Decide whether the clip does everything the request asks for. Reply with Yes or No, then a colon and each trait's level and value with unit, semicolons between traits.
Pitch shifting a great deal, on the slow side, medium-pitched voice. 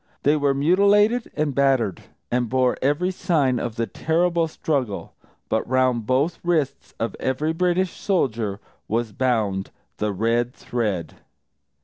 No: wide, 5.8 semitones; slow, 130 wpm; low, 130 Hz